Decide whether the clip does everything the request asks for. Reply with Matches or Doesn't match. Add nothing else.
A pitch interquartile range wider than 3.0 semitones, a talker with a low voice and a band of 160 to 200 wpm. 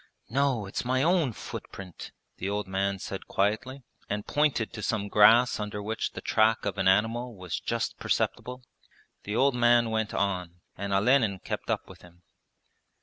Matches